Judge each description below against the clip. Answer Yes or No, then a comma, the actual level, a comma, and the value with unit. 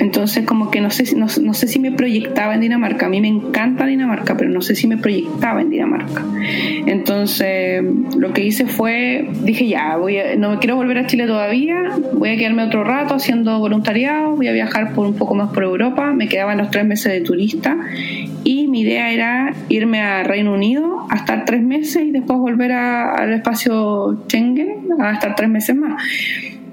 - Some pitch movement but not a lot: Yes, average, 4.2 semitones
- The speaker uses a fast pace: Yes, fast, 200 wpm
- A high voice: Yes, high, 235 Hz